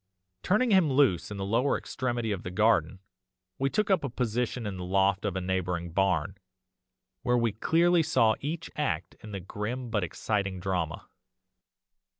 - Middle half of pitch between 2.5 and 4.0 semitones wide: No, wide, 5.6 semitones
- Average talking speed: Yes, average, 165 wpm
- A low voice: Yes, low, 105 Hz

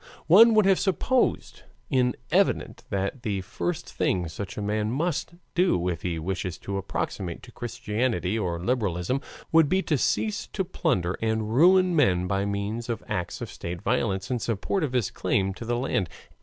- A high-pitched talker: No, low, 110 Hz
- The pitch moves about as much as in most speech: No, wide, 7.4 semitones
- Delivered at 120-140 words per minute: No, average, 175 wpm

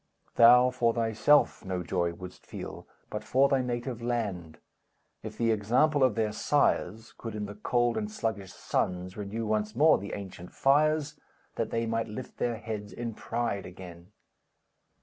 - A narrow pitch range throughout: No, average, 3.5 semitones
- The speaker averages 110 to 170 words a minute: Yes, average, 160 wpm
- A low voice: Yes, low, 115 Hz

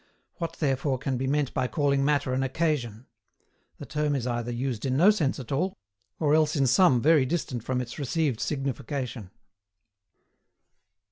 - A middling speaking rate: Yes, average, 160 wpm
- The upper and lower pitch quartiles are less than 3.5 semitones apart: Yes, average, 3.0 semitones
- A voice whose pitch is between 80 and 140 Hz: Yes, low, 135 Hz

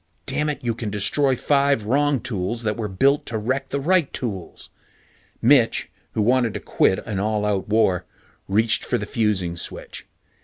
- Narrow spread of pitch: No, average, 4.5 semitones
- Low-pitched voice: Yes, low, 115 Hz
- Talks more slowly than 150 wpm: No, average, 165 wpm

